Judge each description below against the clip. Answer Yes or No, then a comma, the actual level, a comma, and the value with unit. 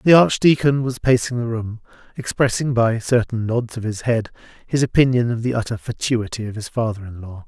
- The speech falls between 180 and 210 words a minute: Yes, average, 195 wpm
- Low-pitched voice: Yes, low, 120 Hz